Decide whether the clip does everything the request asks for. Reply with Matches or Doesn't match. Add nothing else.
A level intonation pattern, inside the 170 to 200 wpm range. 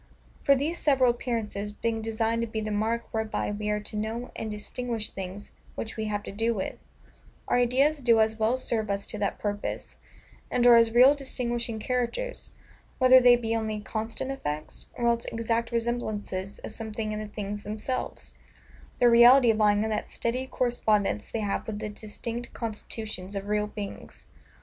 Matches